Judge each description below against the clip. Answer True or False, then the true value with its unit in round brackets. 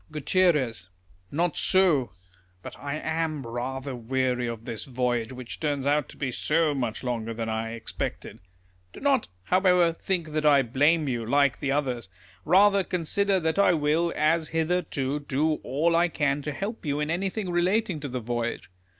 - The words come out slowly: False (165 wpm)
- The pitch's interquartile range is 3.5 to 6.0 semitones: True (4.9 semitones)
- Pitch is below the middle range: False (150 Hz)